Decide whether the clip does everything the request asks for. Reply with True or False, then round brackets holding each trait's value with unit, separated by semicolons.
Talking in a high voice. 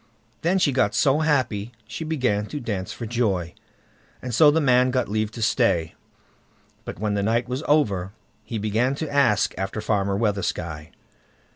False (115 Hz)